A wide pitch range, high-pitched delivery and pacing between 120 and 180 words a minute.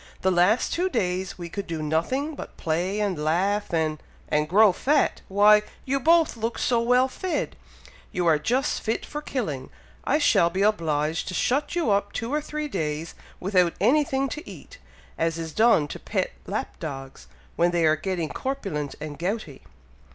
Yes: wide, 7.7 semitones; high, 195 Hz; average, 175 wpm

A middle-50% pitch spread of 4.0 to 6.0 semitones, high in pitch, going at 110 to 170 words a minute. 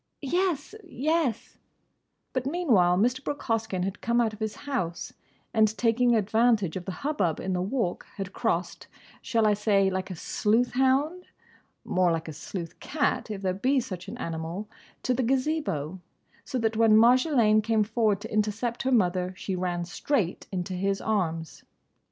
Yes: average, 5.1 semitones; high, 215 Hz; average, 155 wpm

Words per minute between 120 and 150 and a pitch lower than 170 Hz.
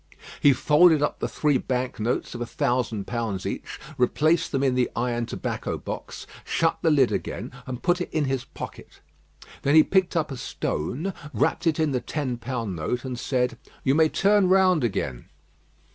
No: average, 185 wpm; low, 135 Hz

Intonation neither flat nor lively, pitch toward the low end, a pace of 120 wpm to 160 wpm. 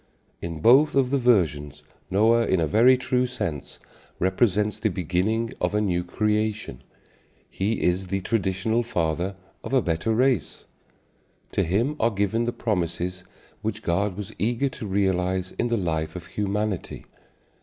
Yes: average, 4.4 semitones; low, 105 Hz; average, 150 wpm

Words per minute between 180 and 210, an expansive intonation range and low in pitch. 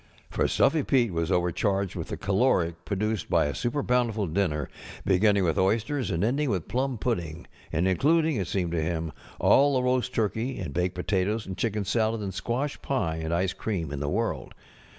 Yes: average, 190 wpm; wide, 5.7 semitones; low, 100 Hz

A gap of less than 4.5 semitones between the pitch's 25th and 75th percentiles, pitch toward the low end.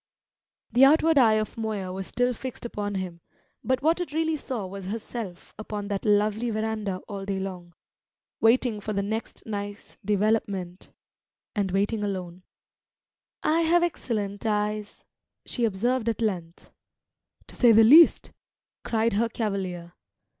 No: average, 3.0 semitones; high, 215 Hz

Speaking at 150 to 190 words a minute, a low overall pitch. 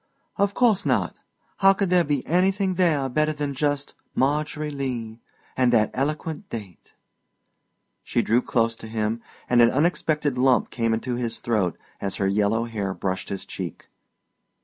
Yes: average, 155 wpm; low, 130 Hz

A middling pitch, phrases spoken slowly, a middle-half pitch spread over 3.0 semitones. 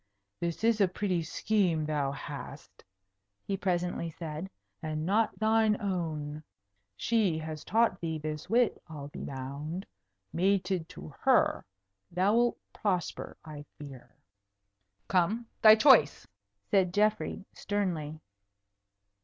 Yes: medium, 175 Hz; slow, 110 wpm; average, 4.9 semitones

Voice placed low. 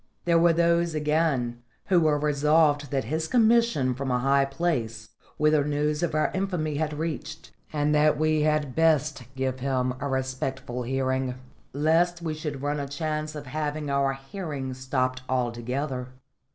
No: medium, 145 Hz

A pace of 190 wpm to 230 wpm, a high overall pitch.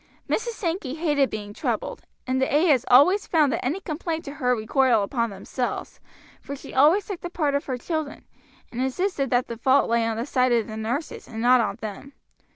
Yes: fast, 205 wpm; very high, 265 Hz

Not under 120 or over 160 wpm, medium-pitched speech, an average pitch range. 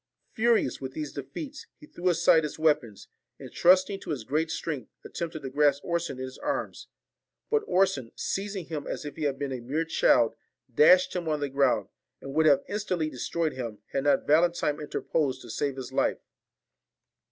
No: average, 185 wpm; medium, 150 Hz; average, 4.0 semitones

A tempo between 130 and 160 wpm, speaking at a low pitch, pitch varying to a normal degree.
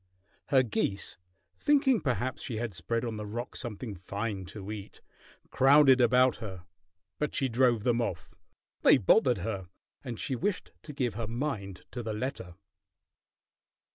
Yes: average, 150 wpm; low, 115 Hz; average, 3.9 semitones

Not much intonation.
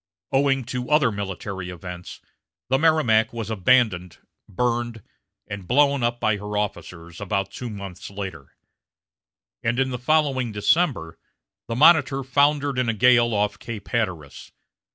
No: average, 4.7 semitones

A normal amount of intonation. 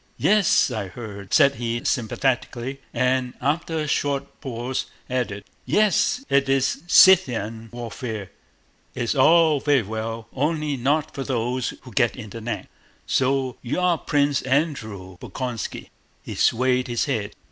Yes: average, 3.7 semitones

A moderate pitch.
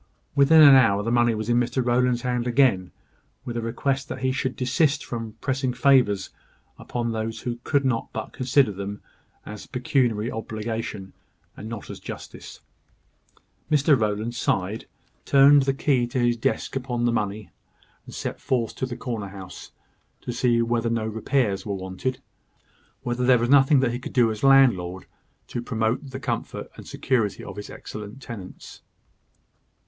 No: low, 120 Hz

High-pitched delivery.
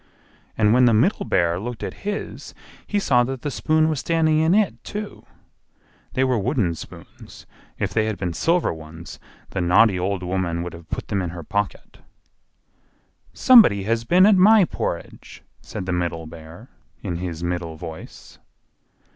No: low, 105 Hz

